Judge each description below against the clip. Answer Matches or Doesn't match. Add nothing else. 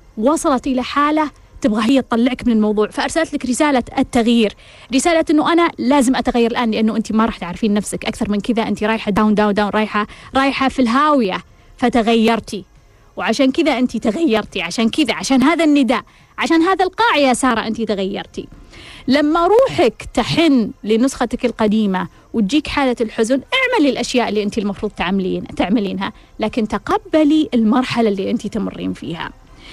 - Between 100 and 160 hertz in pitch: Doesn't match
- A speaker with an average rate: Doesn't match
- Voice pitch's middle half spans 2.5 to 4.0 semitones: Doesn't match